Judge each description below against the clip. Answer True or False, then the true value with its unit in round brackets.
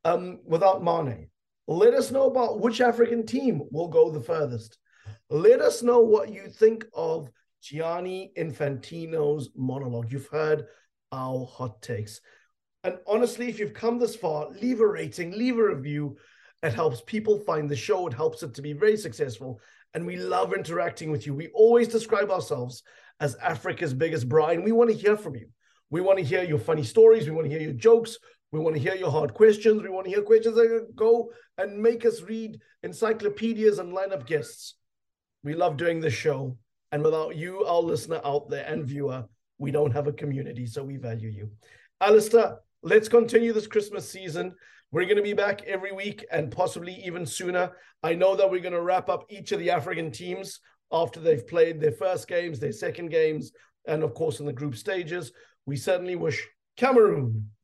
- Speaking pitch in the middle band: True (170 Hz)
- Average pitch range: False (6.9 semitones)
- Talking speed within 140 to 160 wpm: False (190 wpm)